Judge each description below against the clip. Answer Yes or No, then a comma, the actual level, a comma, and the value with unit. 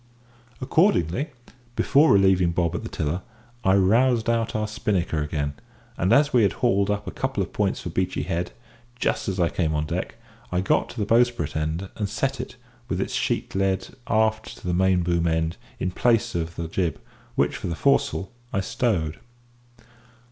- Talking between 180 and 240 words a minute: Yes, average, 185 wpm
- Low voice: Yes, very low, 95 Hz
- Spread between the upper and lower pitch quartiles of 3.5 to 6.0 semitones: Yes, average, 5.1 semitones